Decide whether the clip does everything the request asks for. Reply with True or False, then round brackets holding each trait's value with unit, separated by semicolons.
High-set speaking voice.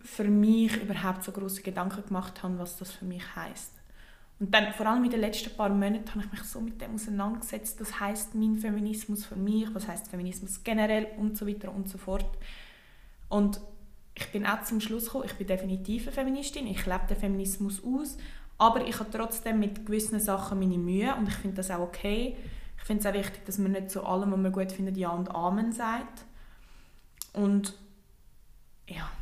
True (205 Hz)